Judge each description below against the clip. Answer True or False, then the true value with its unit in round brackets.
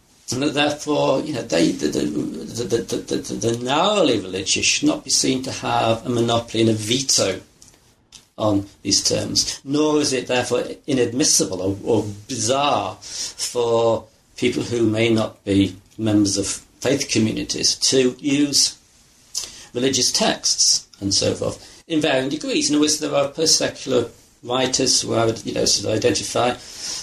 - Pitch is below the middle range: True (120 Hz)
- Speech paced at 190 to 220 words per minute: False (160 wpm)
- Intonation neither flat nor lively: True (4.0 semitones)